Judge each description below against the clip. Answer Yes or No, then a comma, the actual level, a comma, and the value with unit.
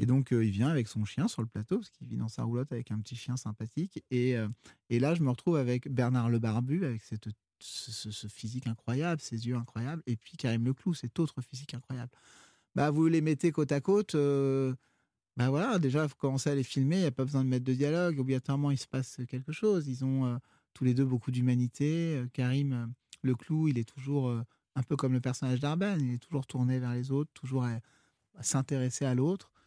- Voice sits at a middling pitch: No, low, 130 Hz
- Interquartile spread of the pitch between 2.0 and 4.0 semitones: Yes, average, 2.9 semitones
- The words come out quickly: Yes, fast, 235 wpm